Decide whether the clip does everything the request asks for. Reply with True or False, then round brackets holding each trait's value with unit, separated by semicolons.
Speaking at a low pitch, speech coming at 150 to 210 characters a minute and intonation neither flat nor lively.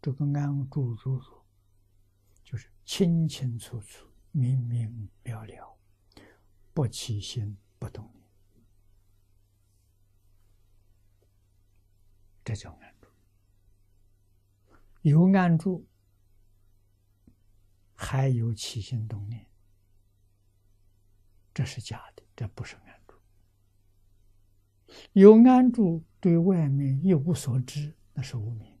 False (100 Hz; 120 characters per minute; 4.0 semitones)